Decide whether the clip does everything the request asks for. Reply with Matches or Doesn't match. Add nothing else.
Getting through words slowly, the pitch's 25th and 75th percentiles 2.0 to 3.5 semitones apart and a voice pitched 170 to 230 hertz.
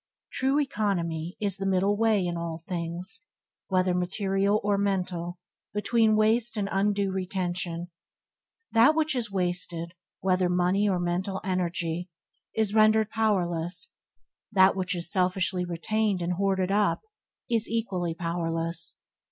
Matches